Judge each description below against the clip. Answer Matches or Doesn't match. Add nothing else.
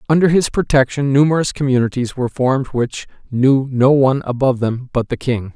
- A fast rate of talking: Doesn't match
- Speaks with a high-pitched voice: Doesn't match